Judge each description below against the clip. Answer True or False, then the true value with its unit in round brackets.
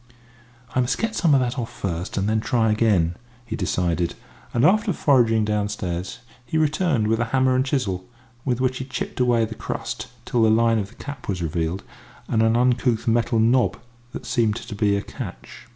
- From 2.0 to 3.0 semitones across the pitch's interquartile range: False (3.8 semitones)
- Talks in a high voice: False (115 Hz)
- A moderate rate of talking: True (195 wpm)